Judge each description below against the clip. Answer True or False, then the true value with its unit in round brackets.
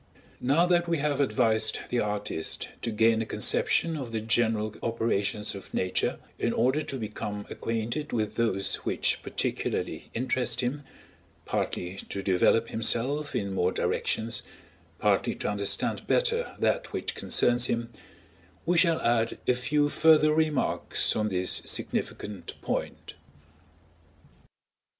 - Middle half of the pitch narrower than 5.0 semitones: False (5.5 semitones)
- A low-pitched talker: True (115 Hz)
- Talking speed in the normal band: False (130 wpm)